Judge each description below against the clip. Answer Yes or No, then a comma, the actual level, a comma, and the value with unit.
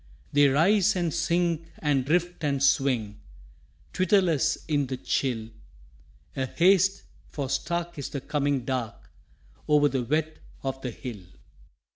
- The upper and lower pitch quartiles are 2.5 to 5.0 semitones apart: Yes, average, 4.3 semitones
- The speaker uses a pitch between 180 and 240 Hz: No, medium, 145 Hz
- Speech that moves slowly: Yes, slow, 130 wpm